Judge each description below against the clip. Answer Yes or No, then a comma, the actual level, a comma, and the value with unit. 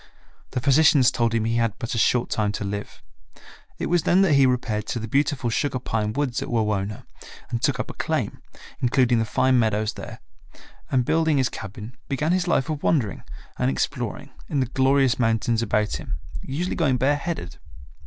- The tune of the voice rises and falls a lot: No, average, 4.0 semitones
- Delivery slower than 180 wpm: No, average, 190 wpm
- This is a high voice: No, low, 125 Hz